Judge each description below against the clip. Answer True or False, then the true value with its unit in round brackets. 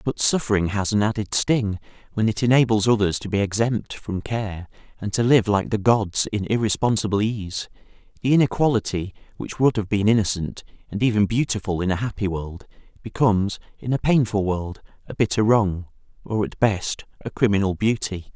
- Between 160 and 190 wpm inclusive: True (170 wpm)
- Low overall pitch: True (105 Hz)